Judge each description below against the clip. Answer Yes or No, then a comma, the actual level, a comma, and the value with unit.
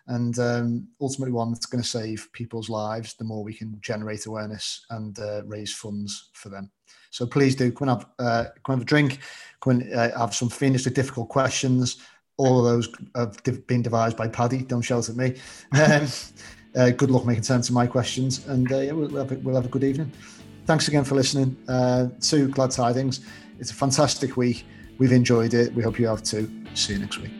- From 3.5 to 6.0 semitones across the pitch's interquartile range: No, narrow, 2.6 semitones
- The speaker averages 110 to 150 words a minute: No, fast, 205 wpm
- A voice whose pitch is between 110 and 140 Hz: Yes, low, 120 Hz